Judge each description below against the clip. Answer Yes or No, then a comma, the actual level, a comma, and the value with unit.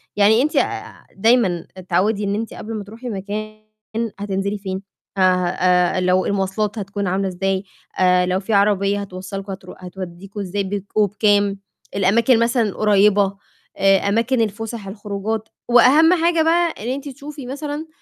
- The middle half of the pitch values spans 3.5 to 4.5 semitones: No, average, 2.8 semitones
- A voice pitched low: No, high, 205 Hz